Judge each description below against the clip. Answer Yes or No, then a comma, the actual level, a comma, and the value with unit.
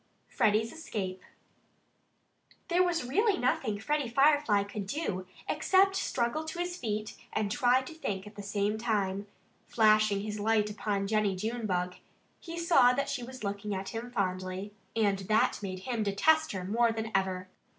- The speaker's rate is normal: Yes, average, 160 wpm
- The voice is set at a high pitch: Yes, high, 215 Hz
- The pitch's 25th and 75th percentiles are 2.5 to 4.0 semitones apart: No, average, 4.5 semitones